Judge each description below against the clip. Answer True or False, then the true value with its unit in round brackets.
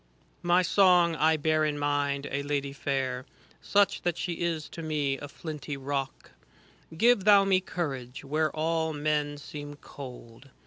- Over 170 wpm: False (155 wpm)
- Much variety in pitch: False (2.9 semitones)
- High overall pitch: False (150 Hz)